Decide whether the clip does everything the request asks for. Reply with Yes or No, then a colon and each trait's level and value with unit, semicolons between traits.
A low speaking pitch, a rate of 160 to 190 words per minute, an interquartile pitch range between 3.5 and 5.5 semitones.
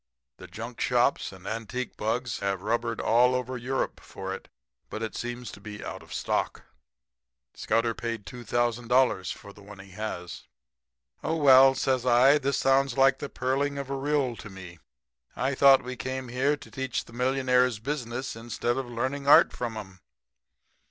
No: low, 125 Hz; average, 165 wpm; average, 3.0 semitones